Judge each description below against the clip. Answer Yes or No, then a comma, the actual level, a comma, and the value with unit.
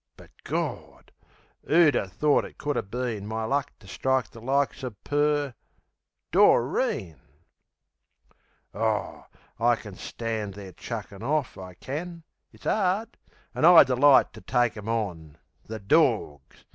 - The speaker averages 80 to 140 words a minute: Yes, slow, 135 wpm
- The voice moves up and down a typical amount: No, wide, 5.9 semitones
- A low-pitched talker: Yes, low, 120 Hz